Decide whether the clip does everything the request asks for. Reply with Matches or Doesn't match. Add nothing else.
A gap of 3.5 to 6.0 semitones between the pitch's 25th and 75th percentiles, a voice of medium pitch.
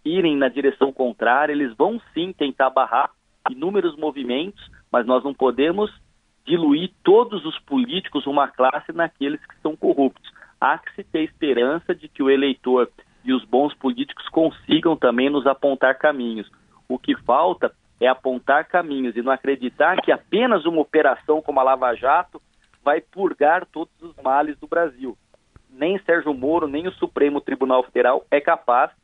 Matches